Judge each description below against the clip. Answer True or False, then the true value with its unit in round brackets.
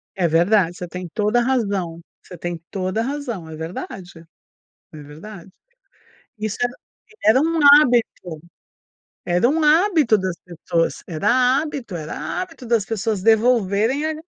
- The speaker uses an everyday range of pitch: False (5.8 semitones)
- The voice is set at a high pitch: True (210 Hz)